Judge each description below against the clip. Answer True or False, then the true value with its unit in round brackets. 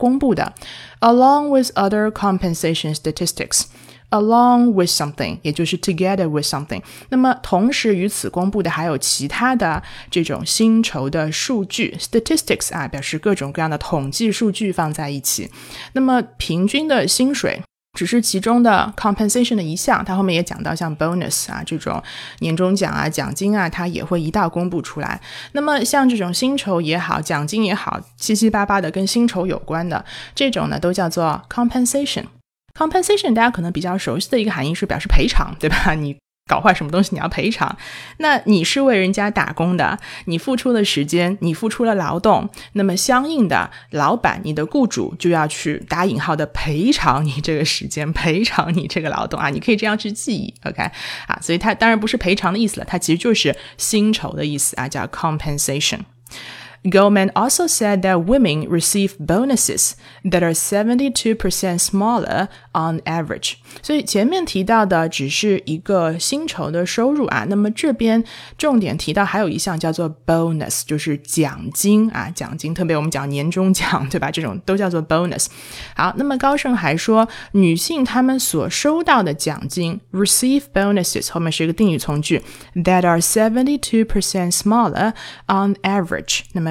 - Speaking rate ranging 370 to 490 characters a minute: True (410 characters per minute)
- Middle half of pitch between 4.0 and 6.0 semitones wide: True (5.5 semitones)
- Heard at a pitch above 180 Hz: True (190 Hz)